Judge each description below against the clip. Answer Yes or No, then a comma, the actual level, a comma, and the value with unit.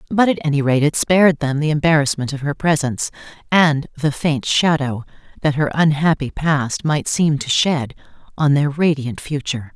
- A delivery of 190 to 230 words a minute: No, average, 170 wpm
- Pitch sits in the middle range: Yes, medium, 150 Hz